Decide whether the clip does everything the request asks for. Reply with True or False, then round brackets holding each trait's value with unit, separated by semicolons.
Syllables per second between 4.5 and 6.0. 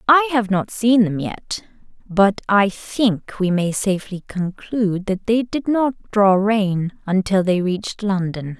False (4.0 syllables/s)